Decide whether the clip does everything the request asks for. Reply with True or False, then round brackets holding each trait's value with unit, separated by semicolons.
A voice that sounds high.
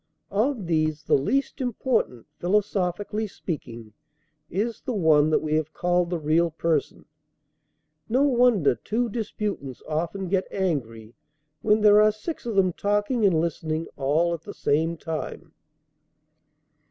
False (175 Hz)